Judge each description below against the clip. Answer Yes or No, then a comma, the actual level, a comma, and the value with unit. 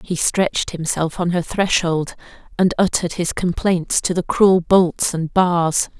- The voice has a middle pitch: Yes, medium, 175 Hz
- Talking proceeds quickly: No, average, 160 wpm